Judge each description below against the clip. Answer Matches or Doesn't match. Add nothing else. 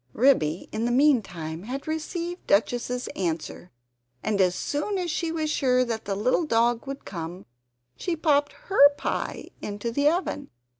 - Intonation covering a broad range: Matches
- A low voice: Doesn't match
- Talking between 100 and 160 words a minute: Matches